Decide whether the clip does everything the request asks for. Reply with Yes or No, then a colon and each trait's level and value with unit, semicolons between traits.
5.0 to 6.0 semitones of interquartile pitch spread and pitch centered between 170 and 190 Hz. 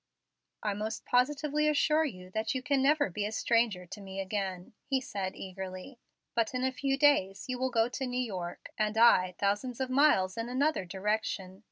No: wide, 5.5 semitones; high, 225 Hz